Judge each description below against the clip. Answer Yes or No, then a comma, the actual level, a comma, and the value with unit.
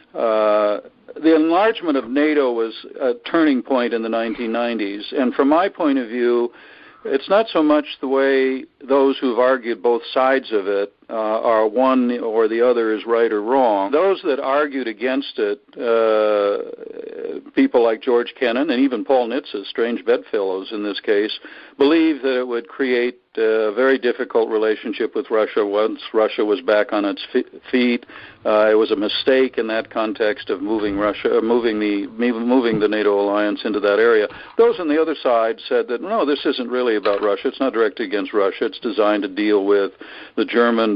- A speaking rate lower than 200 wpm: Yes, average, 190 wpm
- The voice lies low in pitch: Yes, low, 125 Hz